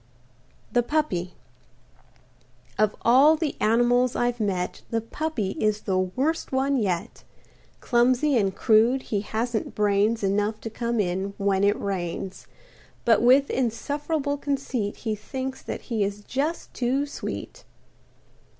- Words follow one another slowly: Yes, slow, 130 wpm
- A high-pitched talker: Yes, high, 230 Hz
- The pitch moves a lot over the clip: No, average, 4.5 semitones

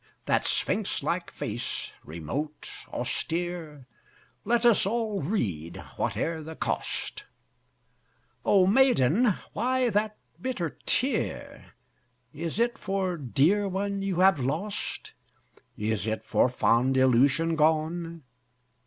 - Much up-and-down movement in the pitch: Yes, wide, 7.1 semitones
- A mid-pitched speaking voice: Yes, medium, 170 Hz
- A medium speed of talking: No, slow, 105 wpm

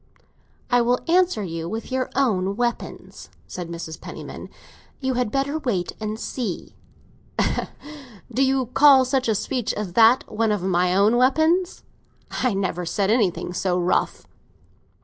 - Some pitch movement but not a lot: No, wide, 5.7 semitones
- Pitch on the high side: Yes, high, 225 Hz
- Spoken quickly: No, average, 145 wpm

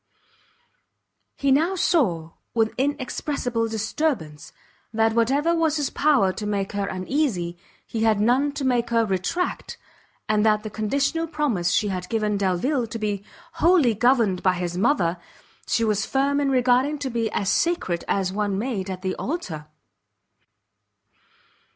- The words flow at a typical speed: Yes, average, 145 wpm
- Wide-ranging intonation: Yes, wide, 6.2 semitones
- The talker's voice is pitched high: Yes, high, 225 Hz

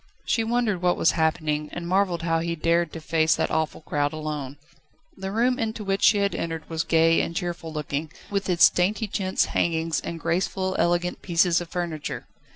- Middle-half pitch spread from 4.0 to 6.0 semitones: No, average, 2.8 semitones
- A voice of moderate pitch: Yes, medium, 170 Hz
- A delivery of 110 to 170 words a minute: No, average, 185 wpm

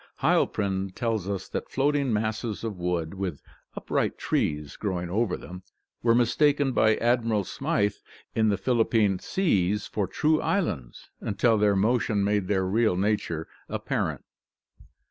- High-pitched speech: No, low, 105 Hz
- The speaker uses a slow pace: No, average, 145 wpm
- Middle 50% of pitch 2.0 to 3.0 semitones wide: No, average, 3.5 semitones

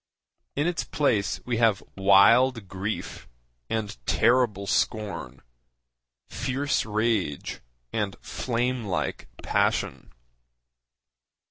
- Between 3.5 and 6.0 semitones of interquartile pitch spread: Yes, average, 3.9 semitones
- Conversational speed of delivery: No, slow, 85 wpm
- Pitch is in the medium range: No, low, 110 Hz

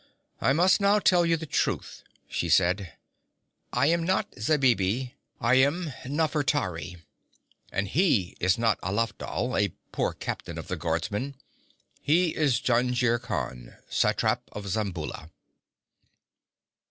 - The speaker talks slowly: Yes, slow, 120 wpm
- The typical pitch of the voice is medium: No, low, 125 Hz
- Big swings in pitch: Yes, wide, 7.7 semitones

